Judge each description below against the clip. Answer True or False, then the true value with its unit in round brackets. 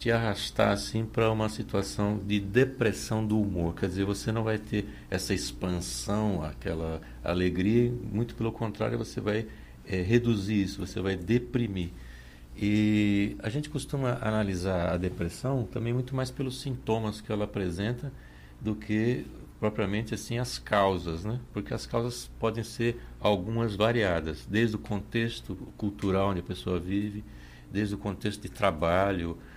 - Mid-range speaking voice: False (105 Hz)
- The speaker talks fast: False (150 wpm)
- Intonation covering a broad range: False (3.3 semitones)